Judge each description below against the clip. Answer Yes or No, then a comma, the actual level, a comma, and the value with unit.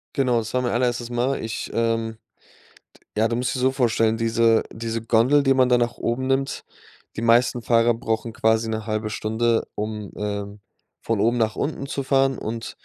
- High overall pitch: No, low, 115 Hz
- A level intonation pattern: Yes, narrow, 2.0 semitones